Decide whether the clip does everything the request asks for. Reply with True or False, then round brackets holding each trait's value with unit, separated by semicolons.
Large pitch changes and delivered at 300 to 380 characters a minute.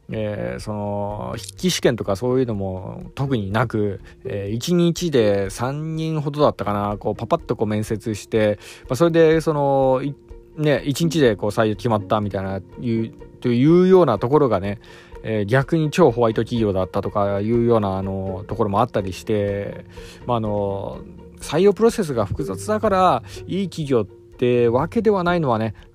True (6.6 semitones; 320 characters per minute)